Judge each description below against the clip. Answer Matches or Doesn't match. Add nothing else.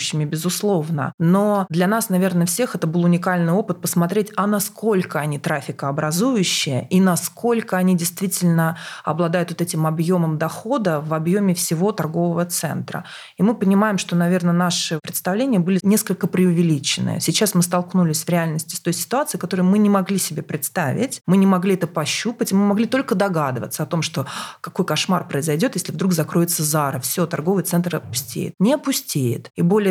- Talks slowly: Doesn't match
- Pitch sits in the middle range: Matches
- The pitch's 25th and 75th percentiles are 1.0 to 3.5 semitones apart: Matches